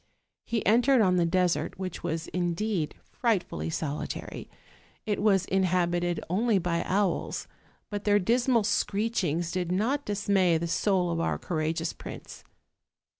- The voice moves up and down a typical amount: Yes, average, 3.4 semitones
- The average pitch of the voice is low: No, medium, 185 Hz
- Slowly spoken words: Yes, slow, 130 wpm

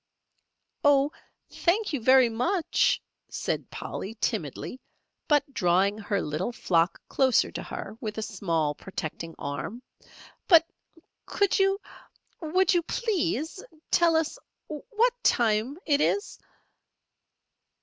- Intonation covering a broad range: Yes, wide, 9.0 semitones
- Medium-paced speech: No, slow, 110 wpm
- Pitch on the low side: No, very high, 260 Hz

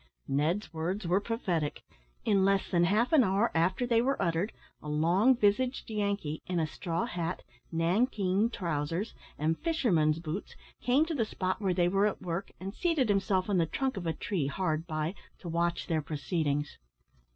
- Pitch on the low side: No, medium, 185 Hz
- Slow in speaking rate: No, average, 175 wpm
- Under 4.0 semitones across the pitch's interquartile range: No, average, 4.3 semitones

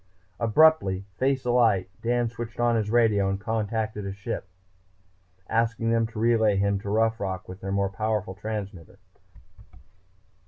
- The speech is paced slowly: No, average, 150 wpm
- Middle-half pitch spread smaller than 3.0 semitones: Yes, narrow, 2.6 semitones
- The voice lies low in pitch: Yes, low, 110 Hz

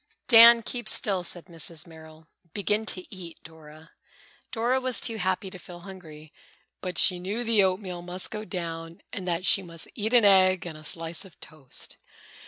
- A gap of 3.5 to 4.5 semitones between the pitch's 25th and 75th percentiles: Yes, average, 4.0 semitones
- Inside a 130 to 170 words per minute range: No, average, 180 wpm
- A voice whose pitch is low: No, medium, 185 Hz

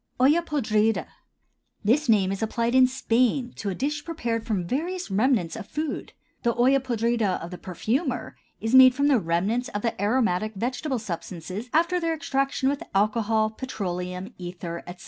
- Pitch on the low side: No, high, 230 Hz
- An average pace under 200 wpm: Yes, average, 165 wpm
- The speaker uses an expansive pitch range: No, average, 4.8 semitones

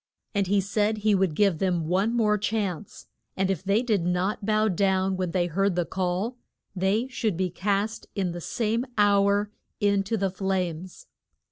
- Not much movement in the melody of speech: Yes, narrow, 2.3 semitones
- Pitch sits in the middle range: No, high, 195 Hz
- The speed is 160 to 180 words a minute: Yes, average, 175 wpm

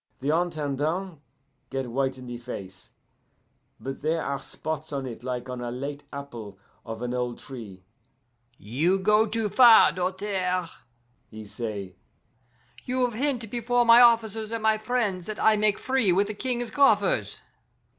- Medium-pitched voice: Yes, medium, 170 Hz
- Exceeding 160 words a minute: No, average, 155 wpm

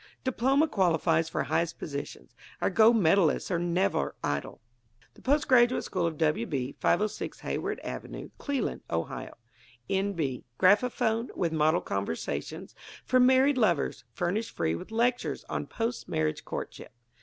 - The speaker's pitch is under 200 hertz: Yes, medium, 185 Hz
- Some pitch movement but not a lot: No, wide, 7.6 semitones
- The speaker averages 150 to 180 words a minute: No, average, 140 wpm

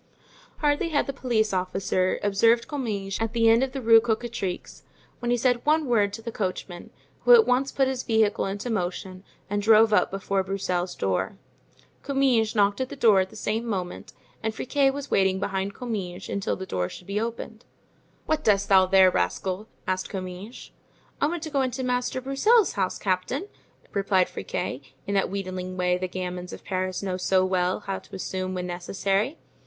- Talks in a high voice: Yes, high, 200 Hz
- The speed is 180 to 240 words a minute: Yes, average, 185 wpm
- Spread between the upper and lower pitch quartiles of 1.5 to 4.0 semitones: No, average, 4.6 semitones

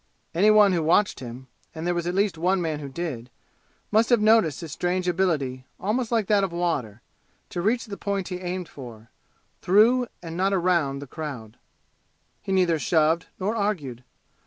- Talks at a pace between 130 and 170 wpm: No, average, 180 wpm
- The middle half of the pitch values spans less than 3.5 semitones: No, average, 4.9 semitones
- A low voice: No, medium, 175 Hz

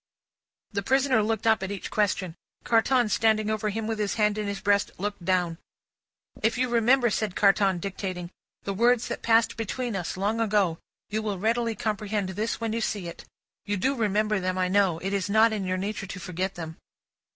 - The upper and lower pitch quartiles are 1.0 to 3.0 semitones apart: Yes, average, 2.7 semitones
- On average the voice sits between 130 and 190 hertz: No, high, 210 Hz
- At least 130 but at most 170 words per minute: No, average, 195 wpm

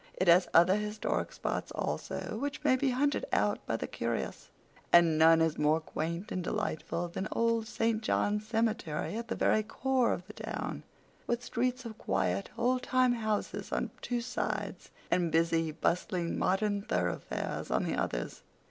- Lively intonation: Yes, wide, 5.9 semitones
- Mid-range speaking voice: No, high, 210 Hz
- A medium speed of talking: Yes, average, 165 wpm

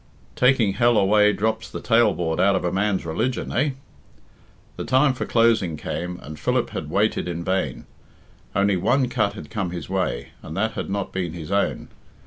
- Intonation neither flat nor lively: Yes, average, 4.3 semitones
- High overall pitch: No, low, 100 Hz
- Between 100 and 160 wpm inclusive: No, average, 180 wpm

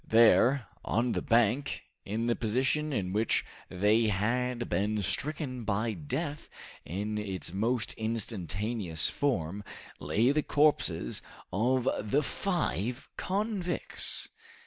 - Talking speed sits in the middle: No, slow, 110 wpm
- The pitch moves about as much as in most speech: Yes, average, 4.3 semitones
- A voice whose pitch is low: Yes, low, 115 Hz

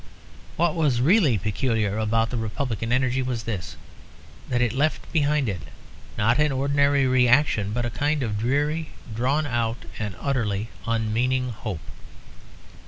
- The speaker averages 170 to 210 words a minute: No, average, 140 wpm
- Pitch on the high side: No, low, 125 Hz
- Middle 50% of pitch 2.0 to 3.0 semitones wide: No, average, 4.0 semitones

